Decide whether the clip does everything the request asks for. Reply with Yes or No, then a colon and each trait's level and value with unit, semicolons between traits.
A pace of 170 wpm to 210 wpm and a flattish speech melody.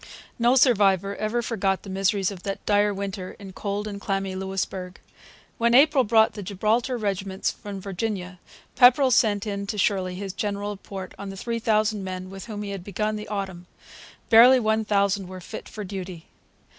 Yes: average, 180 wpm; narrow, 2.1 semitones